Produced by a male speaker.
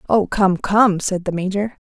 No: female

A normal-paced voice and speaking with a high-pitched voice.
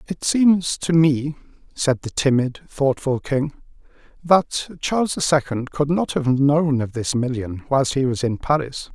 No: average, 170 wpm; medium, 140 Hz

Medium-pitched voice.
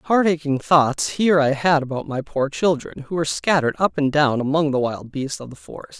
Yes: medium, 145 Hz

